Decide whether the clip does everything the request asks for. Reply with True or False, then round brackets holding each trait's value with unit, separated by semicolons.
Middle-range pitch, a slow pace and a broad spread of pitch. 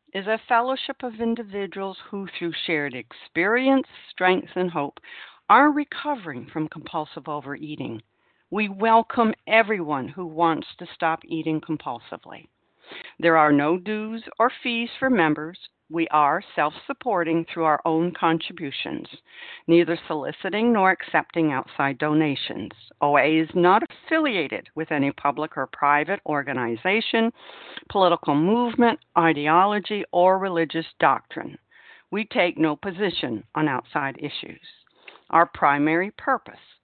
True (170 Hz; 120 wpm; 5.9 semitones)